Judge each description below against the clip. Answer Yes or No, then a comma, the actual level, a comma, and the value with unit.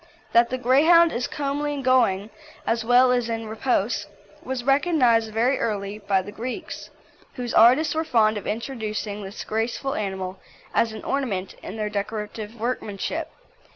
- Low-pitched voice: No, high, 230 Hz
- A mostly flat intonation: No, average, 3.6 semitones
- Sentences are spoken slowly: No, average, 155 wpm